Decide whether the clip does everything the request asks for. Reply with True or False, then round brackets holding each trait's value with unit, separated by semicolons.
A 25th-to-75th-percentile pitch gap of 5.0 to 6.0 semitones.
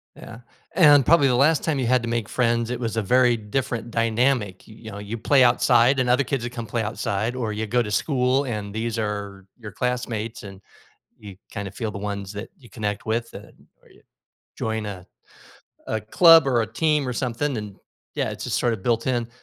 False (3.1 semitones)